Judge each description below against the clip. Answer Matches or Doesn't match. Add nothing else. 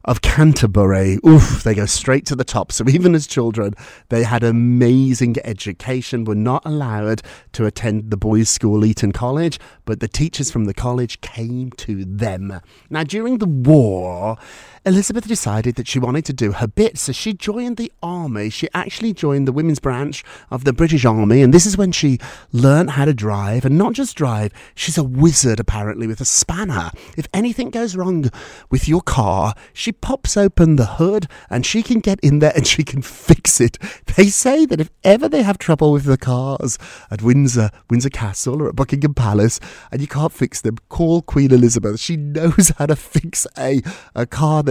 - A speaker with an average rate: Matches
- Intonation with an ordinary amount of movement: Doesn't match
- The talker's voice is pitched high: Doesn't match